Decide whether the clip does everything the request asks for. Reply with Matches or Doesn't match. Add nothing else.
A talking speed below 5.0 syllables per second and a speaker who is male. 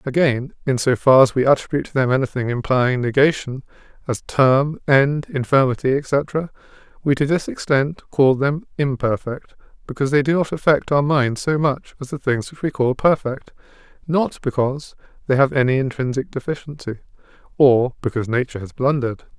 Doesn't match